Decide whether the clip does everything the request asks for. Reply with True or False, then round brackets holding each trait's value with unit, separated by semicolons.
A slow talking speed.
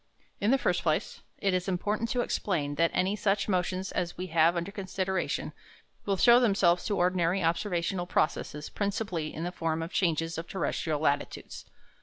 False (170 wpm)